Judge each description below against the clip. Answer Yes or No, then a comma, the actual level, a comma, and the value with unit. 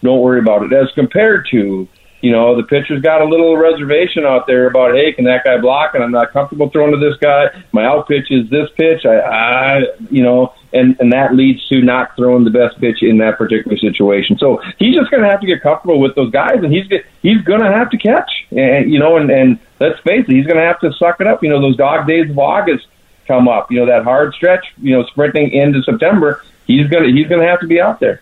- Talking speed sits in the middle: No, fast, 255 wpm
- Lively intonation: No, average, 4.7 semitones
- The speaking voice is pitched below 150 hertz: Yes, medium, 140 Hz